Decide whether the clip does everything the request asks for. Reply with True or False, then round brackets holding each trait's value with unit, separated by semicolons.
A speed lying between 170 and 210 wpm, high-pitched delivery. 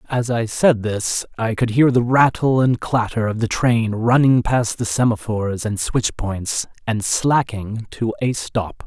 False (175 wpm; 115 Hz)